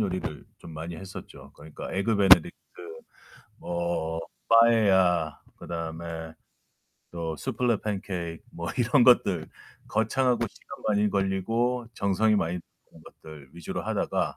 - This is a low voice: Yes, very low, 95 Hz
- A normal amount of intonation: Yes, average, 4.6 semitones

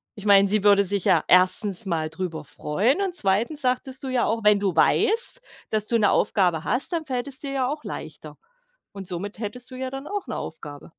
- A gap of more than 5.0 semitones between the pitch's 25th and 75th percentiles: Yes, wide, 5.6 semitones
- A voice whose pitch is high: Yes, high, 210 Hz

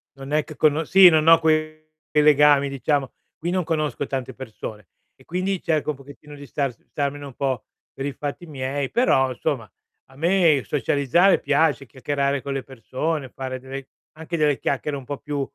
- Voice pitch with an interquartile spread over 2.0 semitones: Yes, narrow, 2.5 semitones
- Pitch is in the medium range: Yes, medium, 145 Hz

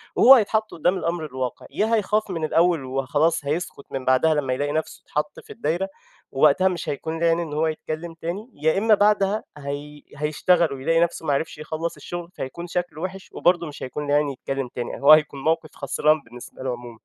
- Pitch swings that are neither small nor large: Yes, average, 3.5 semitones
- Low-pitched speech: No, medium, 155 Hz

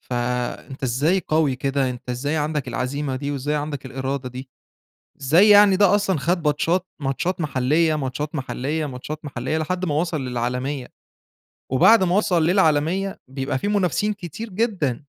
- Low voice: No, medium, 150 Hz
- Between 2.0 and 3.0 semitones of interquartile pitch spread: No, average, 5.2 semitones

